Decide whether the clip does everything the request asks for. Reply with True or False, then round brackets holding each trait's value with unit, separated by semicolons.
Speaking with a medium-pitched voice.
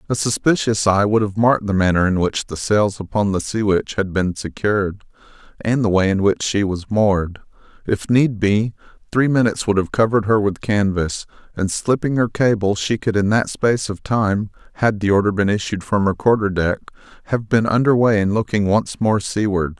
False (105 Hz)